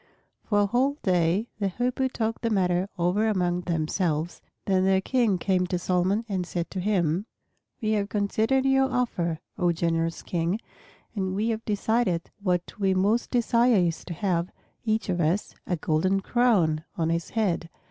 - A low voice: No, high, 190 Hz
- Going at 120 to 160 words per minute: No, average, 170 wpm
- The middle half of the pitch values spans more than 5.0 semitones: No, average, 4.0 semitones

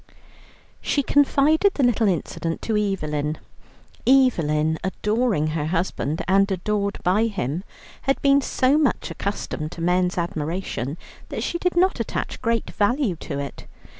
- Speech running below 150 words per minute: Yes, slow, 135 wpm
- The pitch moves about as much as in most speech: No, wide, 7.7 semitones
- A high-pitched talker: Yes, high, 195 Hz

